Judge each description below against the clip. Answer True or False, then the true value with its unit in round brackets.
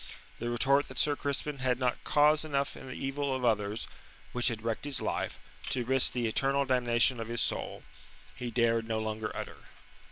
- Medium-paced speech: True (190 wpm)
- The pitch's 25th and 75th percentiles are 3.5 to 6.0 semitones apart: False (3.0 semitones)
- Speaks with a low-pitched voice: True (125 Hz)